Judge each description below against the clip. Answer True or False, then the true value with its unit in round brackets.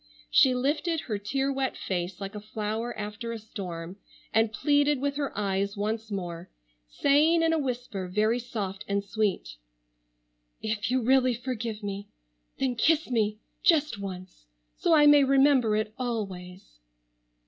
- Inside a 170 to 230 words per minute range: False (150 wpm)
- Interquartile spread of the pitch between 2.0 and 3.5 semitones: False (5.1 semitones)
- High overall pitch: True (220 Hz)